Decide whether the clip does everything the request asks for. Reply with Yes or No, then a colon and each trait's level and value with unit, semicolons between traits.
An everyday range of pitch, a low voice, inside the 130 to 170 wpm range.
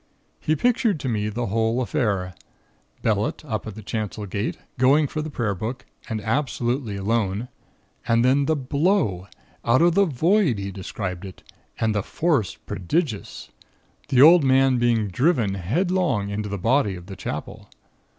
No: wide, 6.0 semitones; low, 115 Hz; average, 160 wpm